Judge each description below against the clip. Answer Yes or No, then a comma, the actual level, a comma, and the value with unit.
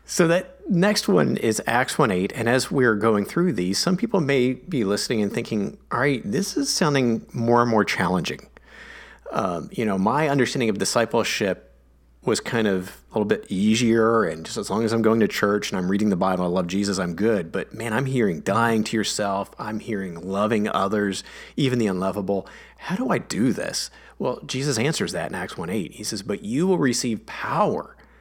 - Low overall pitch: Yes, low, 110 Hz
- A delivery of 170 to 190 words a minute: No, average, 200 wpm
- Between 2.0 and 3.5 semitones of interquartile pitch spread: No, average, 5.1 semitones